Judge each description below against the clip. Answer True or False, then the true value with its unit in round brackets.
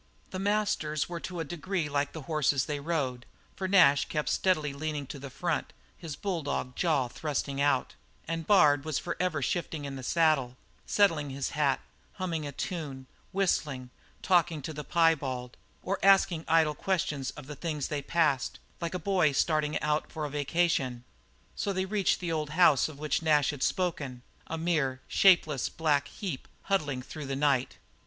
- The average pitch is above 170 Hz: False (155 Hz)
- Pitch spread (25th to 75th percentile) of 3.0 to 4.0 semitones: True (3.5 semitones)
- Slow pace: False (170 wpm)